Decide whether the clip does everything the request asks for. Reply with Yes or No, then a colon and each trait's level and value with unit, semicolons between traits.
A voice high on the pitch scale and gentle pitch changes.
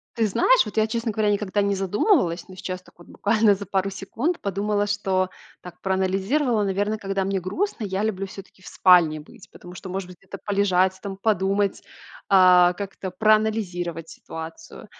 Yes: high, 195 Hz; narrow, 2.3 semitones